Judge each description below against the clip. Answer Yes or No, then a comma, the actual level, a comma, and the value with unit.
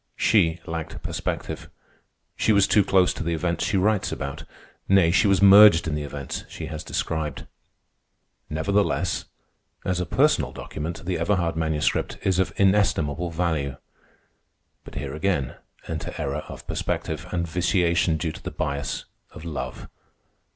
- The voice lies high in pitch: No, very low, 85 Hz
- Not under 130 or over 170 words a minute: Yes, average, 145 wpm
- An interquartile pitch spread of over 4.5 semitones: No, average, 3.4 semitones